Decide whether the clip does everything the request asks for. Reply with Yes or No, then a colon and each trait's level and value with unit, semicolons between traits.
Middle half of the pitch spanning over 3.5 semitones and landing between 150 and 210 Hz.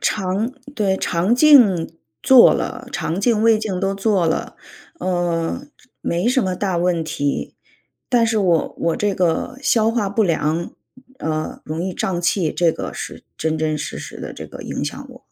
Yes: average, 4.7 semitones; medium, 185 Hz